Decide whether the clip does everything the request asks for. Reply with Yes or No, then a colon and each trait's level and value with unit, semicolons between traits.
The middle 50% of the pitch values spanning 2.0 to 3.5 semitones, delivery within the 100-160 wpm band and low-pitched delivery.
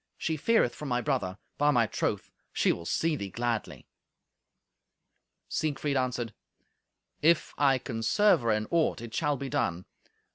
No: average, 4.5 semitones; average, 150 wpm; low, 130 Hz